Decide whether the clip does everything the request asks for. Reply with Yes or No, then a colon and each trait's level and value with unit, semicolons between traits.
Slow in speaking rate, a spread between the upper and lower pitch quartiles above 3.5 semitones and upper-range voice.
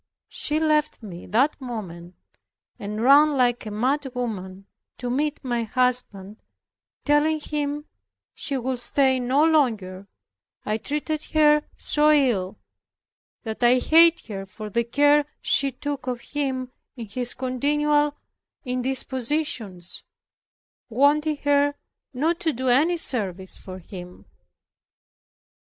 Yes: slow, 120 wpm; average, 5.0 semitones; very high, 255 Hz